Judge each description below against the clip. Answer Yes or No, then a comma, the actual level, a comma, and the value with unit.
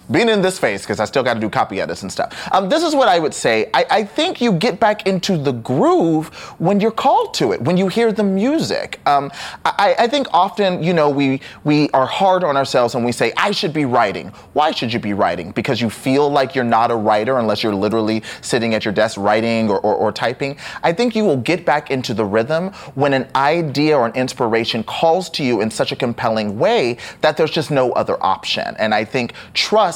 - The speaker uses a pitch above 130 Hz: Yes, medium, 140 Hz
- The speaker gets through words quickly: Yes, fast, 235 wpm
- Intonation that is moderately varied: No, wide, 8.3 semitones